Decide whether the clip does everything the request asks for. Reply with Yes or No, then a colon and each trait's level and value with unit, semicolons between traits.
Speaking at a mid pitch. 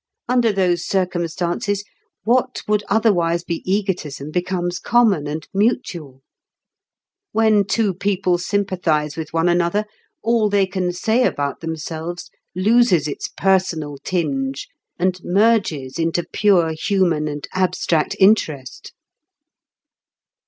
Yes: medium, 180 Hz